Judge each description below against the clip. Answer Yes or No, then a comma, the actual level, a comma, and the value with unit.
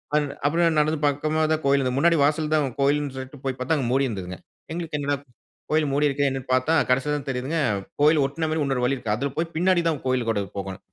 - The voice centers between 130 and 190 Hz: Yes, medium, 140 Hz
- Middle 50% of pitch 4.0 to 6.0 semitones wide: No, average, 3.1 semitones